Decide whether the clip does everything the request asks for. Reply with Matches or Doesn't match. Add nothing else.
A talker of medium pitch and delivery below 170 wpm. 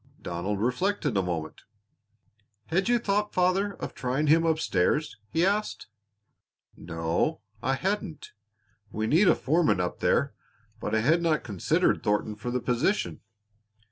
Matches